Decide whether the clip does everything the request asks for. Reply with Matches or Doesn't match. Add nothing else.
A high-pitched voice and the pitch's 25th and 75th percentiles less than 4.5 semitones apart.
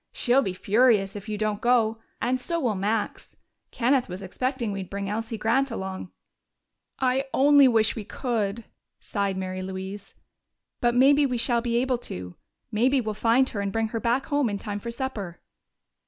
Matches